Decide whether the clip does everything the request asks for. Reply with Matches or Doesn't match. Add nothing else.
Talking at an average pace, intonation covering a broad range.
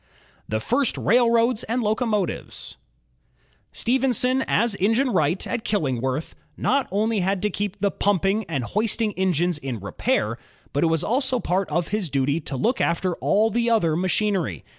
Matches